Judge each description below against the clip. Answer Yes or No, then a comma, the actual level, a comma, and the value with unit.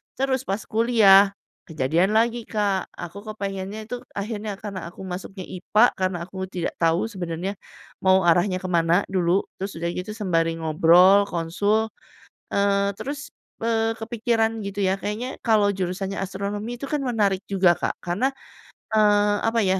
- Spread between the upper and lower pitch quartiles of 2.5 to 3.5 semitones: Yes, average, 3.0 semitones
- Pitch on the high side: Yes, high, 200 Hz